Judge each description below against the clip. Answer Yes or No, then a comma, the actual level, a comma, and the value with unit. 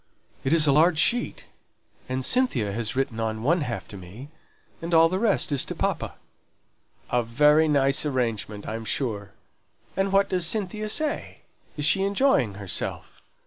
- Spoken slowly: No, average, 160 wpm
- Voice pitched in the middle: Yes, medium, 145 Hz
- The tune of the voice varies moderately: No, wide, 7.9 semitones